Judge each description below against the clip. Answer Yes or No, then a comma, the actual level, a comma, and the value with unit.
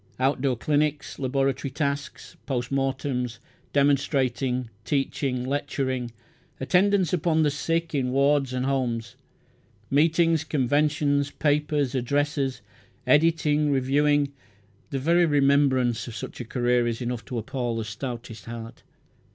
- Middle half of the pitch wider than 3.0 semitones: No, average, 2.7 semitones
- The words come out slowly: Yes, slow, 115 wpm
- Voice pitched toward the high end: No, low, 135 Hz